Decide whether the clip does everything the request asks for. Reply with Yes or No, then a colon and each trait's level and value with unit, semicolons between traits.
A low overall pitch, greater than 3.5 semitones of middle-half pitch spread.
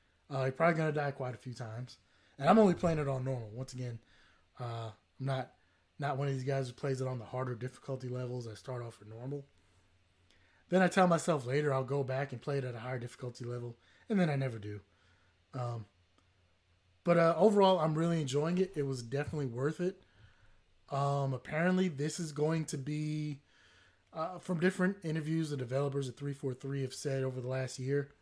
Yes: low, 130 Hz; average, 4.2 semitones